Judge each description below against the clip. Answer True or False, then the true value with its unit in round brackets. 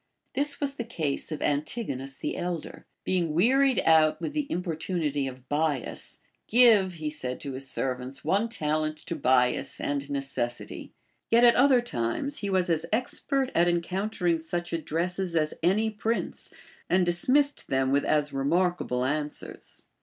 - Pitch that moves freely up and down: True (6.8 semitones)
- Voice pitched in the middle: True (165 Hz)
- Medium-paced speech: True (155 wpm)